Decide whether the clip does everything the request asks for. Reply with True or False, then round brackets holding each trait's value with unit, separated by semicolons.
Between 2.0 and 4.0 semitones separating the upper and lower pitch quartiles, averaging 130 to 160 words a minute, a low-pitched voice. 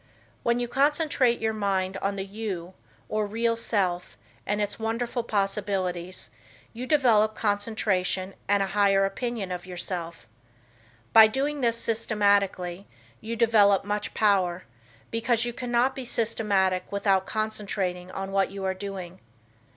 False (3.2 semitones; 135 wpm; 205 Hz)